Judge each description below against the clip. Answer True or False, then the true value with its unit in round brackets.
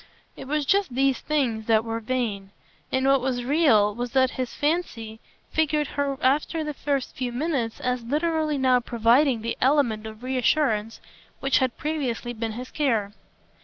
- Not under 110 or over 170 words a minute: True (165 wpm)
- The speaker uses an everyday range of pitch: True (4.1 semitones)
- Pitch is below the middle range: False (255 Hz)